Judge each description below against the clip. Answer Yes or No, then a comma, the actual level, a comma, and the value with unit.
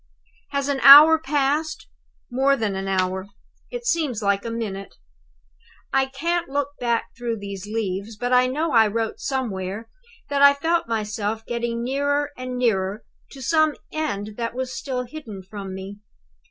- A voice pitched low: No, high, 240 Hz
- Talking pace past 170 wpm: No, average, 155 wpm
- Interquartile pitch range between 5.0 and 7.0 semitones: Yes, wide, 5.4 semitones